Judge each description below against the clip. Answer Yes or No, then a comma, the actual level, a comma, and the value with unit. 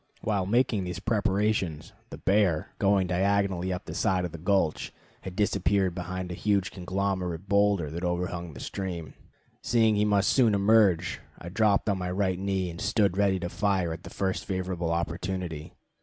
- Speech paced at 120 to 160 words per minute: No, average, 170 wpm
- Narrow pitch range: Yes, narrow, 2.2 semitones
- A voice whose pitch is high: No, very low, 95 Hz